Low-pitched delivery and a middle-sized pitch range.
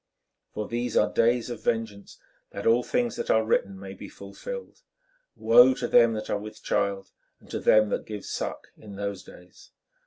Yes: low, 110 Hz; average, 3.0 semitones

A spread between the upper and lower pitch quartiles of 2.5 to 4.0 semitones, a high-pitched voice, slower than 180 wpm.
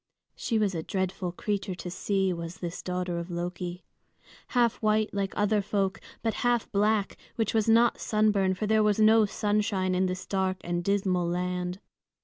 Yes: average, 2.8 semitones; high, 195 Hz; average, 170 wpm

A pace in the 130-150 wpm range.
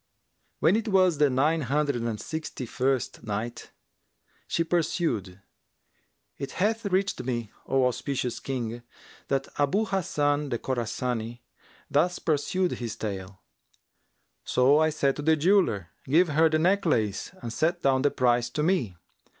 Yes: average, 140 wpm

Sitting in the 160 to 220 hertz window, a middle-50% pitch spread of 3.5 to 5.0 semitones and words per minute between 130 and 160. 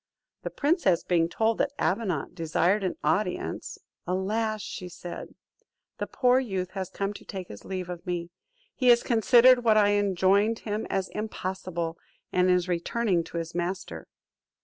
Yes: high, 190 Hz; average, 3.8 semitones; average, 155 wpm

